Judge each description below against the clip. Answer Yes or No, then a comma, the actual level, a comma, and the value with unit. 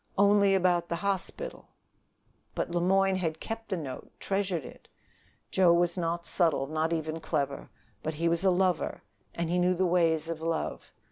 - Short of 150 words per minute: No, average, 175 wpm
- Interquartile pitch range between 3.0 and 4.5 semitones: No, narrow, 2.5 semitones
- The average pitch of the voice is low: No, medium, 175 Hz